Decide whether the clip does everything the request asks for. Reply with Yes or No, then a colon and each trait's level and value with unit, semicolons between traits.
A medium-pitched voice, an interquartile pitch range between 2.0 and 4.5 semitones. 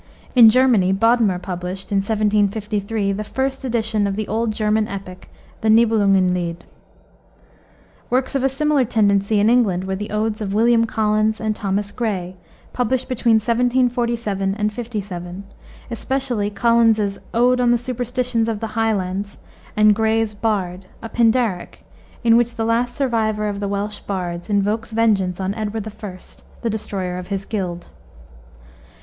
No: high, 215 Hz; average, 2.8 semitones